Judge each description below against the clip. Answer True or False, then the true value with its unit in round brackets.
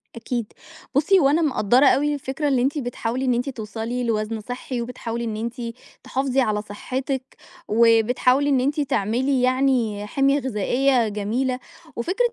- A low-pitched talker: False (250 Hz)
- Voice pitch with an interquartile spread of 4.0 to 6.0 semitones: False (3.1 semitones)